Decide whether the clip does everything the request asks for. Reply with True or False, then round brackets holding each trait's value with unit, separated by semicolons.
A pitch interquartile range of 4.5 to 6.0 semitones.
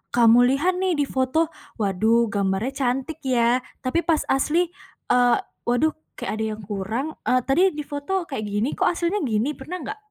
True (5.3 semitones)